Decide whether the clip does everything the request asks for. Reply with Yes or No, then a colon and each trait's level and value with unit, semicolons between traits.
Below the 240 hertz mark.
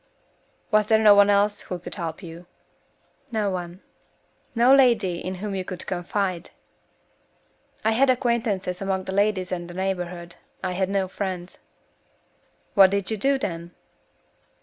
Yes: high, 190 Hz